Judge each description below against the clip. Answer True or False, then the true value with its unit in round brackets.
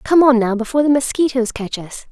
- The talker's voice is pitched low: False (250 Hz)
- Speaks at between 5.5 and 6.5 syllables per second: True (6.0 syllables/s)